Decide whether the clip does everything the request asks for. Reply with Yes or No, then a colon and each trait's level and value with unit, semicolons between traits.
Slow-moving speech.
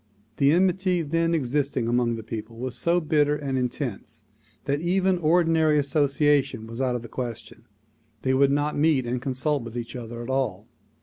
No: average, 175 wpm